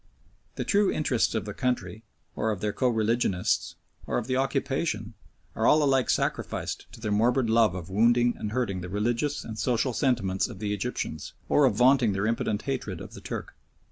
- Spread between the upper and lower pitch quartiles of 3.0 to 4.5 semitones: Yes, average, 3.7 semitones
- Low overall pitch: Yes, low, 115 Hz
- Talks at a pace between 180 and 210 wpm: Yes, average, 190 wpm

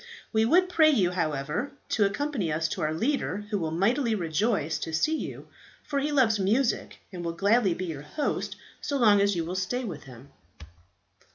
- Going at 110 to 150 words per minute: No, average, 190 wpm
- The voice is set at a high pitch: Yes, high, 200 Hz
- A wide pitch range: Yes, wide, 7.3 semitones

